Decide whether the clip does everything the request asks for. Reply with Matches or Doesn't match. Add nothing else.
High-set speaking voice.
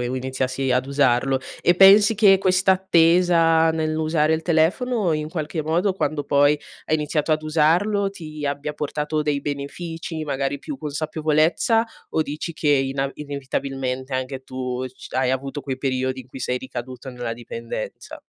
Doesn't match